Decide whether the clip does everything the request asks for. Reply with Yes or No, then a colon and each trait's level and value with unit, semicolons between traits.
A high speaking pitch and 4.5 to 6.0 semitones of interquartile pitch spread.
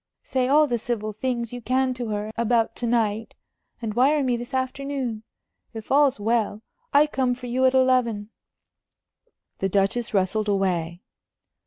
No: high, 240 Hz; average, 3.3 semitones